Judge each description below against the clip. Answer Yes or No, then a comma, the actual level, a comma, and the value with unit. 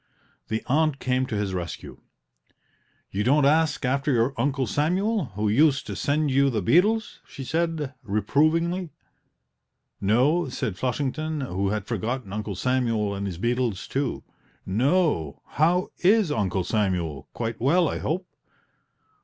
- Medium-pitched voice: No, low, 130 Hz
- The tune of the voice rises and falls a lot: Yes, wide, 6.6 semitones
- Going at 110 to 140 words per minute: Yes, slow, 135 wpm